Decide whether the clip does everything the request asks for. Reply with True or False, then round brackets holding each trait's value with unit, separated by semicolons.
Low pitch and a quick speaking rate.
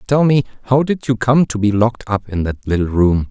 True (115 Hz; 255 wpm)